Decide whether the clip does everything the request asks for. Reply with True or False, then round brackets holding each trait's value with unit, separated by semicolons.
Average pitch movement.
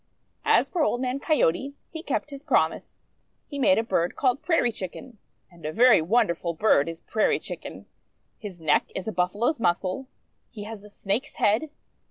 False (6.9 semitones)